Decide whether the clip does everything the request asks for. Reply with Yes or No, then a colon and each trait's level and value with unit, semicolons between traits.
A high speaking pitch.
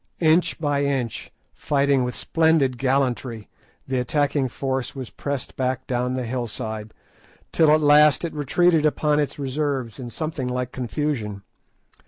No: low, 135 Hz